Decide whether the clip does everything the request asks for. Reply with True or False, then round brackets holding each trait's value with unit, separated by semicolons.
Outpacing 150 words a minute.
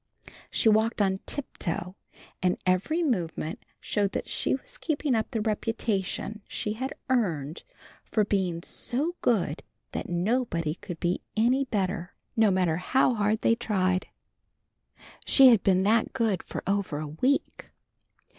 False (140 wpm)